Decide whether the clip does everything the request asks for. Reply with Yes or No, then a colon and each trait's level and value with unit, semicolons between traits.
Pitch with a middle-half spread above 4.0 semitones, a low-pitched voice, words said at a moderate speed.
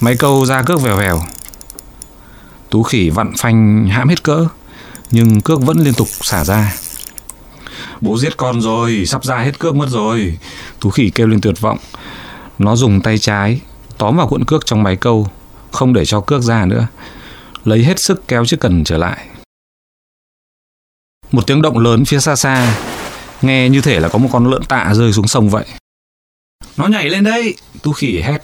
Yes: average, 4.4 semitones; low, 115 Hz; average, 185 wpm